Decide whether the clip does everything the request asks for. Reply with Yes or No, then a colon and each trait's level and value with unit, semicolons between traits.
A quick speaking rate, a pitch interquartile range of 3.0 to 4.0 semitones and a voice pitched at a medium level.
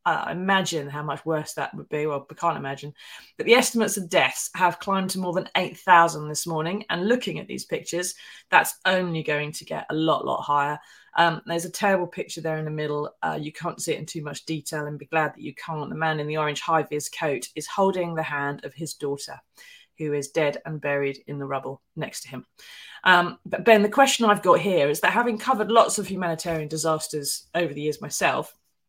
Yes: fast, 230 wpm; average, 3.6 semitones; medium, 160 Hz